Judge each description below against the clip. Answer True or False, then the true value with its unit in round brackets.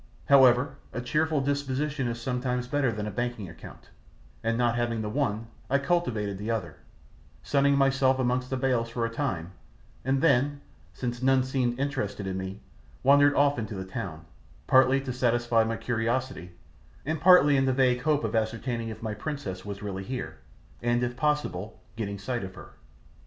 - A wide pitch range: False (3.6 semitones)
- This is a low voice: True (125 Hz)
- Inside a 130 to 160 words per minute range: False (175 wpm)